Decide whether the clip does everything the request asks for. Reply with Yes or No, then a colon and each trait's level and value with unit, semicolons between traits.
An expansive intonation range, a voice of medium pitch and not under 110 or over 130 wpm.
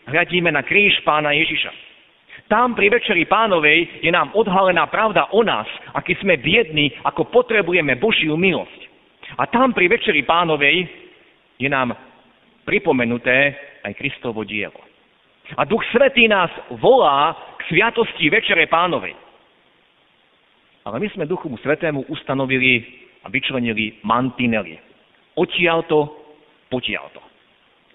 Yes: wide, 6.2 semitones; medium, 155 Hz; average, 115 wpm